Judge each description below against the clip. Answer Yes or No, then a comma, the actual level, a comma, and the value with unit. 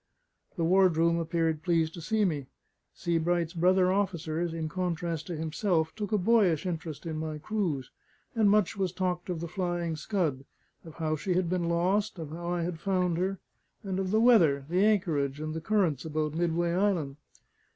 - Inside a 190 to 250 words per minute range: No, average, 180 wpm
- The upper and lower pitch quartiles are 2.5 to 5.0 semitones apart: Yes, average, 2.8 semitones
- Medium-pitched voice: Yes, medium, 170 Hz